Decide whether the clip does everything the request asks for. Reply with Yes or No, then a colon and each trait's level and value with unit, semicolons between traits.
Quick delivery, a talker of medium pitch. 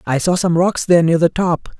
Yes: fast, 265 wpm; medium, 170 Hz